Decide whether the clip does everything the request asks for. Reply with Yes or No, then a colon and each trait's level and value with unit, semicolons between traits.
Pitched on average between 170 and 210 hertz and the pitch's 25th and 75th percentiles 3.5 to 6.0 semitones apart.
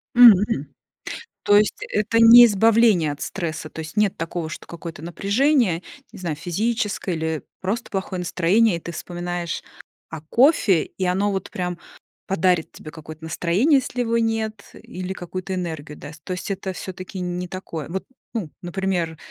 Yes: medium, 185 Hz; average, 3.9 semitones